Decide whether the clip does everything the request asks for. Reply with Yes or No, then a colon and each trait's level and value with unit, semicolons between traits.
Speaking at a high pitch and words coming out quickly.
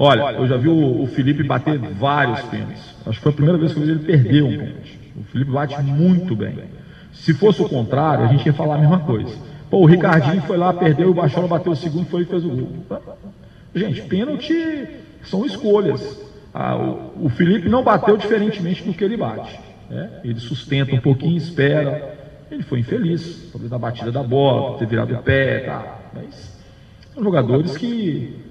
No: medium, 150 Hz; fast, 190 wpm